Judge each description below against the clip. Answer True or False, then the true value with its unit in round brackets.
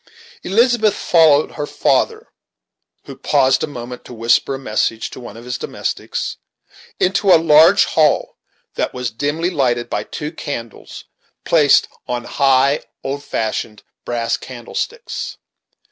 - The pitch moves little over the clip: False (5.0 semitones)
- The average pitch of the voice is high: False (140 Hz)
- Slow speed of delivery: True (130 wpm)